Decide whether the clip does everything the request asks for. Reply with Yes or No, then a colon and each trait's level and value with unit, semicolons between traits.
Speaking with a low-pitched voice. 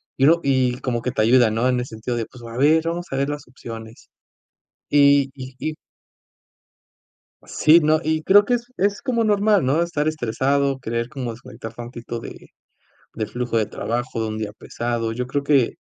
Yes: low, 130 Hz